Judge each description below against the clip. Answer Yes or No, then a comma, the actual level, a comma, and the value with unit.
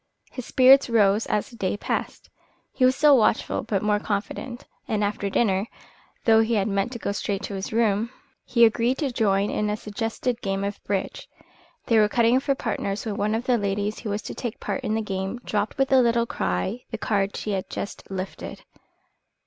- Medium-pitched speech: No, high, 215 Hz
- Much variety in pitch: No, average, 2.7 semitones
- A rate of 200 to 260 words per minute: Yes, fast, 205 wpm